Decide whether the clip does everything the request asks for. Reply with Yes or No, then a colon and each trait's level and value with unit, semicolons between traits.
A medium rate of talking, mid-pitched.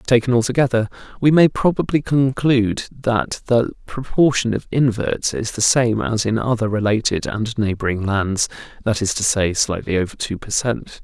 No: average, 165 wpm; low, 115 Hz